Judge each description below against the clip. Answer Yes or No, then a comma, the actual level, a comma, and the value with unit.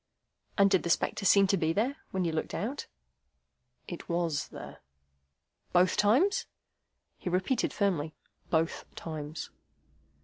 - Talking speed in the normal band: No, slow, 130 wpm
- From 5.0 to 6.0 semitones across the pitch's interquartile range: No, average, 3.7 semitones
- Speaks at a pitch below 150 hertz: No, medium, 180 Hz